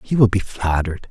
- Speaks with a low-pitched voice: Yes, low, 100 Hz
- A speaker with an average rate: No, fast, 215 wpm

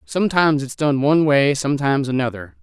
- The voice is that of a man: Yes, male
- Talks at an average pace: Yes, average, 160 wpm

